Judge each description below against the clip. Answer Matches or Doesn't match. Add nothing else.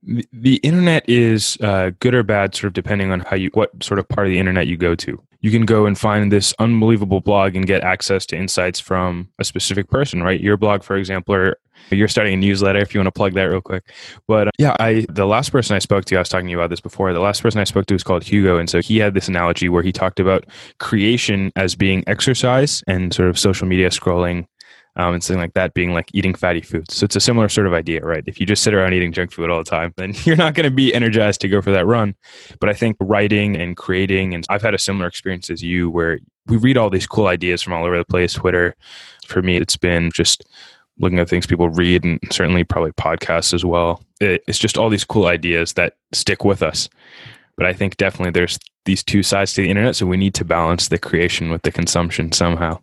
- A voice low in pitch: Matches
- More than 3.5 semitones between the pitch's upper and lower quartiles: Doesn't match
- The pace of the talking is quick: Matches